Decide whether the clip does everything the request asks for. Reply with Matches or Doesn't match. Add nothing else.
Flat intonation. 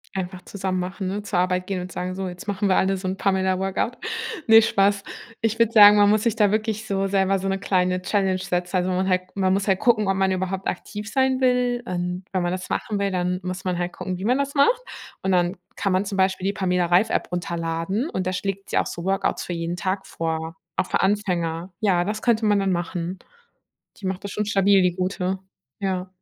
Matches